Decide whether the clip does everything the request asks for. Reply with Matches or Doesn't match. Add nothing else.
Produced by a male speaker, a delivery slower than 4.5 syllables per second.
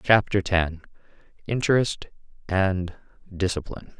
Matches